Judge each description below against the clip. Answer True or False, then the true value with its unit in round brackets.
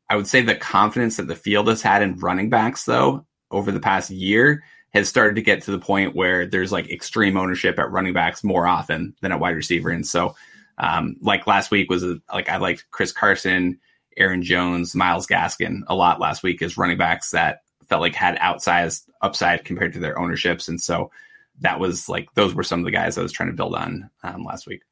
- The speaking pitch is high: False (95 Hz)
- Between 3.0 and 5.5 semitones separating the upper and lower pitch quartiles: False (2.5 semitones)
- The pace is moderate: False (225 wpm)